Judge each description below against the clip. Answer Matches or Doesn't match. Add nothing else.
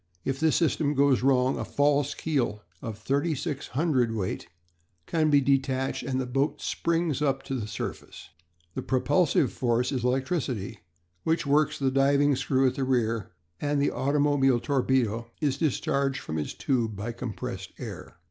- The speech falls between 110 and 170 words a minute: Matches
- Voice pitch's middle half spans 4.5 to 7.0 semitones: Doesn't match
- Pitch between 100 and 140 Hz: Matches